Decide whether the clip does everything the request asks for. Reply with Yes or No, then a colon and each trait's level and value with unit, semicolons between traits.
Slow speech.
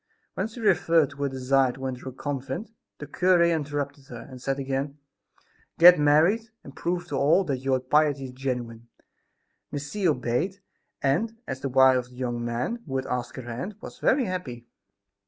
No: average, 185 wpm